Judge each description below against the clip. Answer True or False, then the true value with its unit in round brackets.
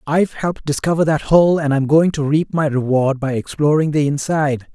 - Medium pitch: True (150 Hz)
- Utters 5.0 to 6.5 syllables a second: True (5.5 syllables/s)